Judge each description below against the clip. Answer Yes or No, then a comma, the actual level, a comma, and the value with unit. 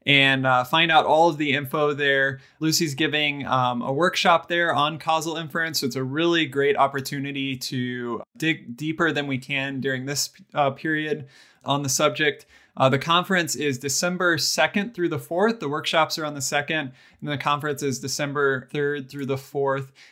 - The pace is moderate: Yes, average, 180 wpm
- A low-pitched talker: No, medium, 145 Hz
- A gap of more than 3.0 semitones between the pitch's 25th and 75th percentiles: No, average, 2.7 semitones